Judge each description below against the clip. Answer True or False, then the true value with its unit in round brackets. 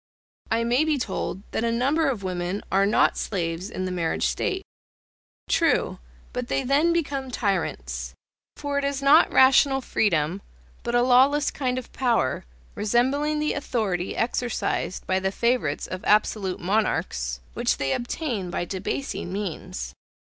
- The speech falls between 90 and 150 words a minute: True (145 wpm)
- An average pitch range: False (6.6 semitones)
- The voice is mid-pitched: False (225 Hz)